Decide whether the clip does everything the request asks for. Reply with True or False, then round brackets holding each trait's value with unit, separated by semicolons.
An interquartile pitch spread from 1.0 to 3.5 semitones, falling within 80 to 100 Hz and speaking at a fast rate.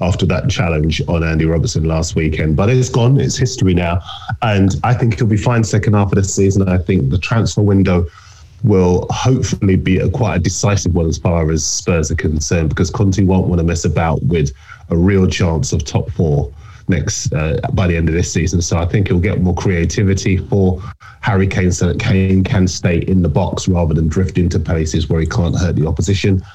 True (3.2 semitones; 95 Hz; 215 wpm)